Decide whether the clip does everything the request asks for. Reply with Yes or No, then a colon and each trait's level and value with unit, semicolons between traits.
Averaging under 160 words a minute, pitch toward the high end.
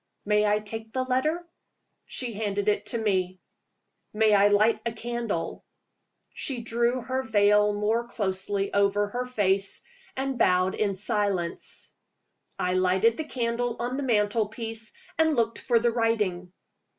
Yes: average, 145 wpm; high, 220 Hz